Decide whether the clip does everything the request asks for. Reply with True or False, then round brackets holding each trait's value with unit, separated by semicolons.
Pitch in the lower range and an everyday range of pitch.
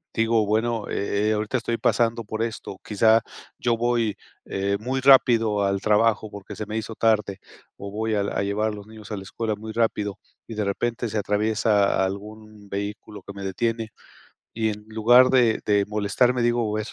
False (110 Hz; 1.9 semitones)